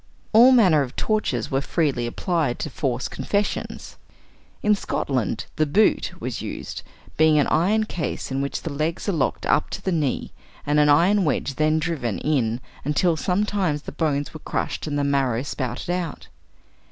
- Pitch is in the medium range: Yes, medium, 155 Hz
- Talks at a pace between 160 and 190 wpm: Yes, average, 170 wpm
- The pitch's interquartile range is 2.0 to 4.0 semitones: No, average, 4.5 semitones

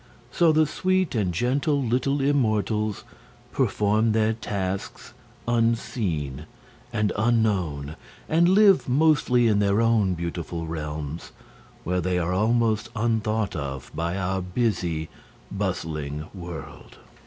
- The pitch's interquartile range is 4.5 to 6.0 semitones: Yes, wide, 5.6 semitones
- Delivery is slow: Yes, slow, 110 wpm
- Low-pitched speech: Yes, low, 105 Hz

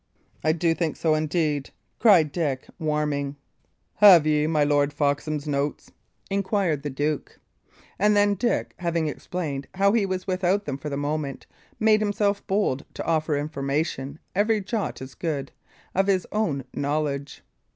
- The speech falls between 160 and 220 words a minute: No, average, 150 wpm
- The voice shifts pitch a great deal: No, average, 5.0 semitones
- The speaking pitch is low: No, medium, 155 Hz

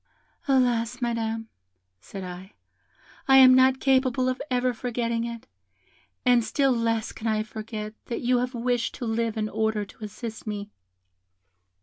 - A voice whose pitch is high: Yes, high, 230 Hz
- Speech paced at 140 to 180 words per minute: Yes, average, 145 wpm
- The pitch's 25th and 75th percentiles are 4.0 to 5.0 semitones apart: No, narrow, 2.4 semitones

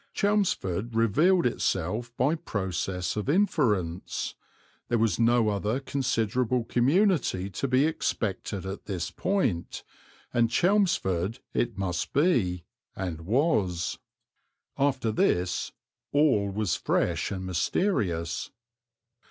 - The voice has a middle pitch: No, low, 110 Hz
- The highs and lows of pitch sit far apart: Yes, wide, 6.9 semitones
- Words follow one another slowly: Yes, slow, 105 wpm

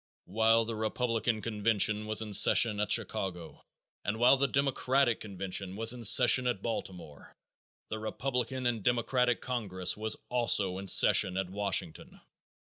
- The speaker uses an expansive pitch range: No, average, 3.6 semitones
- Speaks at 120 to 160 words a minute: Yes, average, 145 wpm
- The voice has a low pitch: Yes, low, 110 Hz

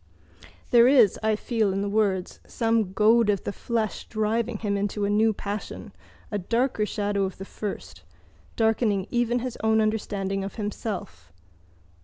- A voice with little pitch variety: Yes, narrow, 2.1 semitones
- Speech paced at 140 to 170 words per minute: Yes, average, 155 wpm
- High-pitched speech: Yes, high, 215 Hz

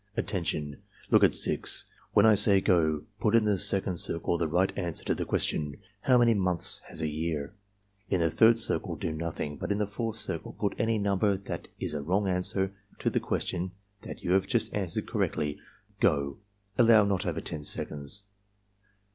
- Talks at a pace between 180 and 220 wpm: Yes, average, 190 wpm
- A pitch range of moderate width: Yes, average, 4.6 semitones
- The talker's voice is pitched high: No, very low, 95 Hz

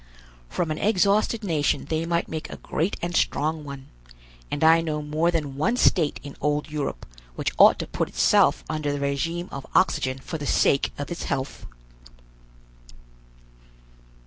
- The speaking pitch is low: No, medium, 155 Hz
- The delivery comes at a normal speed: Yes, average, 160 wpm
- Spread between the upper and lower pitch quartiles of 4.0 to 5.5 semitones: No, average, 2.9 semitones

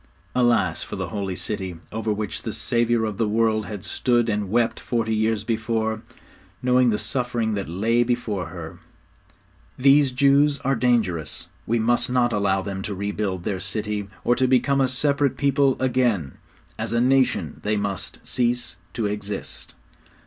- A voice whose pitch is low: Yes, low, 110 Hz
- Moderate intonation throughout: Yes, average, 3.3 semitones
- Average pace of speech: Yes, average, 160 wpm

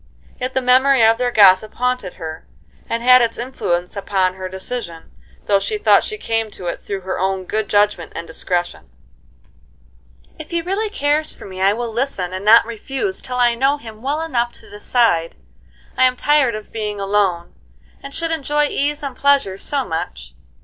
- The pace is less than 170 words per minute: No, average, 180 wpm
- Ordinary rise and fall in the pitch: No, wide, 6.0 semitones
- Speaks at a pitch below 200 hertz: No, high, 230 Hz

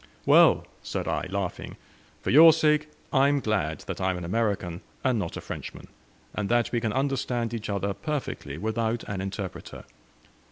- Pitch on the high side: No, low, 110 Hz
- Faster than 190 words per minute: No, average, 170 wpm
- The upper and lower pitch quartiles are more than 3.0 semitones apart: Yes, wide, 5.4 semitones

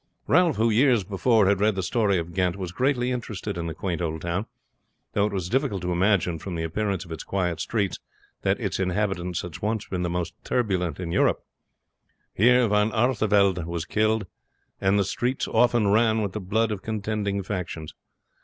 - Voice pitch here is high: No, low, 100 Hz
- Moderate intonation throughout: Yes, average, 3.6 semitones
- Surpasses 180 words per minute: Yes, average, 190 wpm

